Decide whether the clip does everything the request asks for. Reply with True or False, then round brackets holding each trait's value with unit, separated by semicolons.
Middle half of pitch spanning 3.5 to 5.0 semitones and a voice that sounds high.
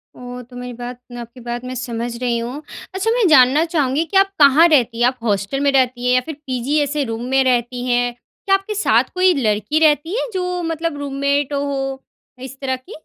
True (4.0 semitones; 265 Hz)